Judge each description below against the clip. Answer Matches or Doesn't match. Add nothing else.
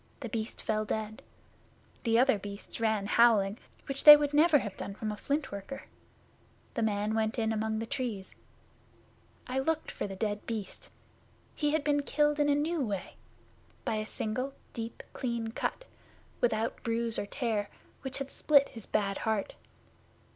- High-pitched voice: Matches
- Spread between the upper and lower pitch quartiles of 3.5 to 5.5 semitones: Matches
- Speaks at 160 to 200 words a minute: Matches